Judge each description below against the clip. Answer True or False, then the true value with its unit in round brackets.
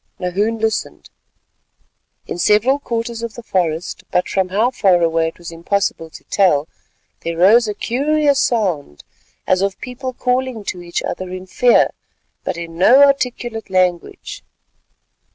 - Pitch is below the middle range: False (200 Hz)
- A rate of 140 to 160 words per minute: True (145 wpm)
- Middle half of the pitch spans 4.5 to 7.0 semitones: True (5.3 semitones)